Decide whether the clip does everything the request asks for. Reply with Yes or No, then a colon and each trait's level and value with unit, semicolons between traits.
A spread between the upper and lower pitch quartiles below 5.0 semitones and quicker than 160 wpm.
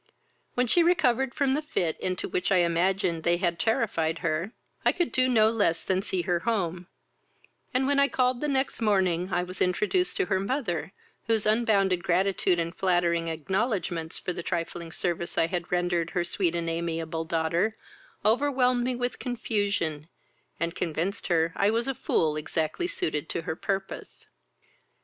No: wide, 5.4 semitones; average, 170 wpm